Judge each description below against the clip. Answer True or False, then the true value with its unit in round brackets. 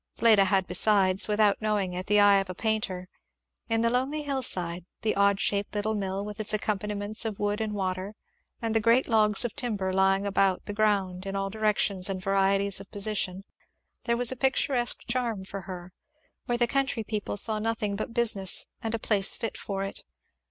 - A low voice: False (205 Hz)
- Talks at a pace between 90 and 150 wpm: False (190 wpm)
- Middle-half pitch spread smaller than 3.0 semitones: True (2.4 semitones)